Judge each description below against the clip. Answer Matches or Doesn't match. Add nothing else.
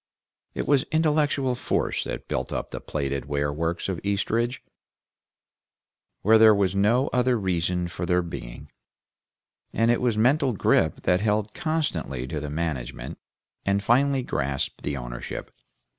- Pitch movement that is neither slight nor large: Doesn't match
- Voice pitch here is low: Matches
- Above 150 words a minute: Doesn't match